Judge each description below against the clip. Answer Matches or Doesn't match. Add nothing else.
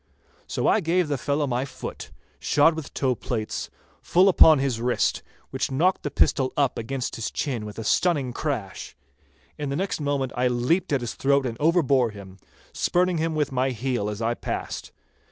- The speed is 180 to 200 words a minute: Matches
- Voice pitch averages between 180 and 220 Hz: Doesn't match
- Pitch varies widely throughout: Doesn't match